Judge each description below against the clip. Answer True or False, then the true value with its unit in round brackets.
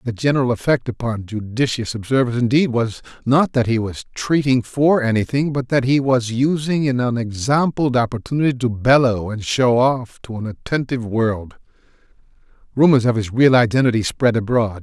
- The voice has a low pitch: True (125 Hz)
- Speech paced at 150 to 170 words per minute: True (160 wpm)